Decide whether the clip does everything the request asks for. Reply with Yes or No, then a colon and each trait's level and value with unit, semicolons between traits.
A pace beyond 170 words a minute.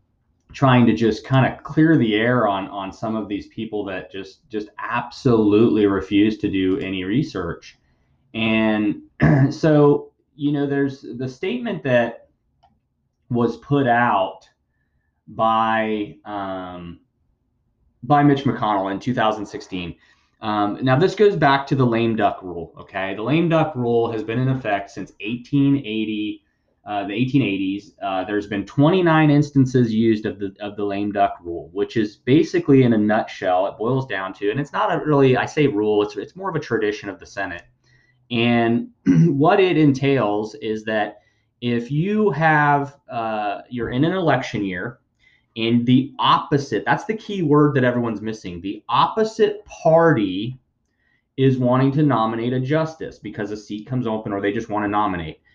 No: average, 160 wpm